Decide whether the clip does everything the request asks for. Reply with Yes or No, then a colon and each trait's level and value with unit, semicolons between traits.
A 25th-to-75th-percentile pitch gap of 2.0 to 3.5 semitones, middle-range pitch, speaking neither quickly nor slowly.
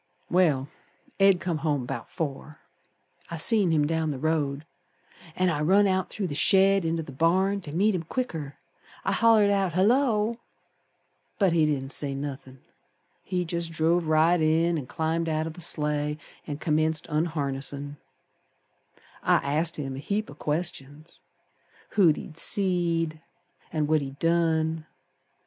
Yes: average, 3.2 semitones; medium, 160 Hz; average, 150 wpm